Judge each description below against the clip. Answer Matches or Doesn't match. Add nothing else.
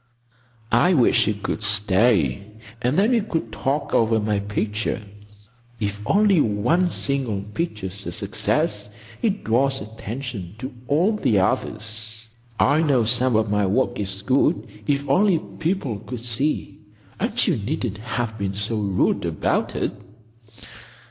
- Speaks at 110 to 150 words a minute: Matches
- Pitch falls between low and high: Doesn't match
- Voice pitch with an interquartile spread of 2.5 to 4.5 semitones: Doesn't match